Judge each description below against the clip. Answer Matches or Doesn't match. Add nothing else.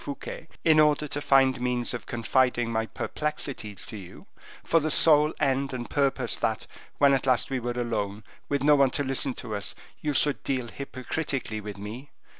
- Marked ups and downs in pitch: Doesn't match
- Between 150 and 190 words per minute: Matches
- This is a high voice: Doesn't match